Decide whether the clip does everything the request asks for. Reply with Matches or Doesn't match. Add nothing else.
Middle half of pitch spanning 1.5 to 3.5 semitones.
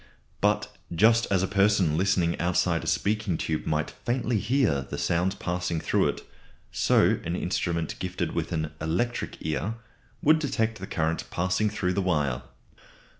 Doesn't match